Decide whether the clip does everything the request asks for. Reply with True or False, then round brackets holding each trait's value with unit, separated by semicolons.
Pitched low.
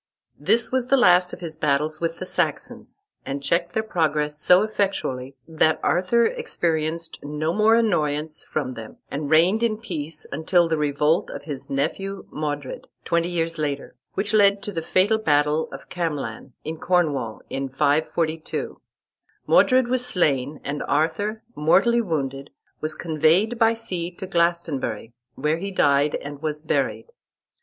False (160 Hz)